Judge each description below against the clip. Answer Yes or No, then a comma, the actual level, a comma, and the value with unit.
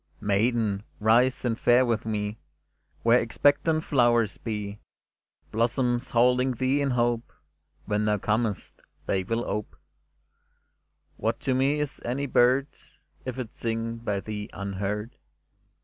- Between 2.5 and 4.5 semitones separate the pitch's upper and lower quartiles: Yes, average, 3.0 semitones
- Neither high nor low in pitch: No, low, 115 Hz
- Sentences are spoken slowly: Yes, slow, 130 wpm